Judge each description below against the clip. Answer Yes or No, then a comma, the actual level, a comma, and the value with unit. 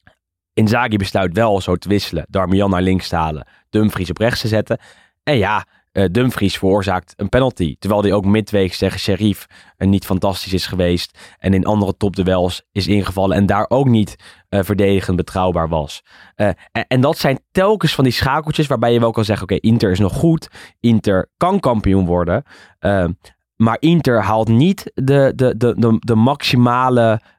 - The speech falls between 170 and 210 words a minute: Yes, average, 180 wpm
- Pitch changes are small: No, average, 3.8 semitones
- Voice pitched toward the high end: No, low, 105 Hz